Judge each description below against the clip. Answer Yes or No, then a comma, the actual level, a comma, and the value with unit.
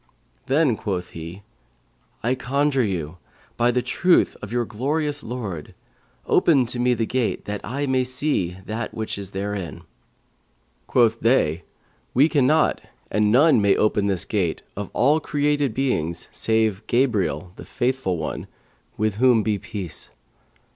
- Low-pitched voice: Yes, low, 115 Hz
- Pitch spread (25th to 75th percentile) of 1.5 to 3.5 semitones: No, average, 4.8 semitones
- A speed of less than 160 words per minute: Yes, average, 140 wpm